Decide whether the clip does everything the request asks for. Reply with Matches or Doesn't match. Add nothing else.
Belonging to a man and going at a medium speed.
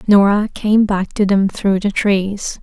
Doesn't match